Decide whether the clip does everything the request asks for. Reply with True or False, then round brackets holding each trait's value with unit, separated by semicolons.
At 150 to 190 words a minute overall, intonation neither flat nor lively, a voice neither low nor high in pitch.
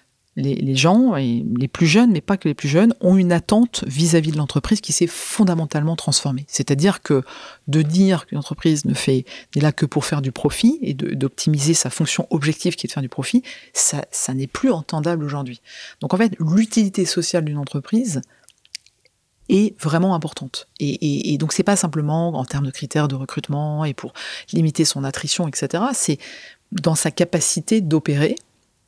True (185 wpm; 4.1 semitones; 160 Hz)